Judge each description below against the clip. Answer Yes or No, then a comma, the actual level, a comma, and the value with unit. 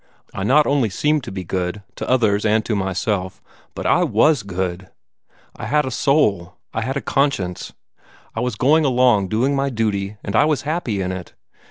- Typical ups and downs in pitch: No, wide, 6.3 semitones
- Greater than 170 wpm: Yes, average, 190 wpm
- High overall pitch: No, low, 110 Hz